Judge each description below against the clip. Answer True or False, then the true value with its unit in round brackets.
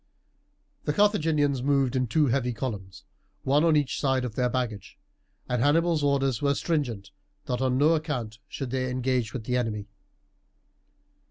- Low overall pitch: True (130 Hz)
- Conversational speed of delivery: True (155 wpm)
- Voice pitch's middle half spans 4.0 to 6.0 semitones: False (3.1 semitones)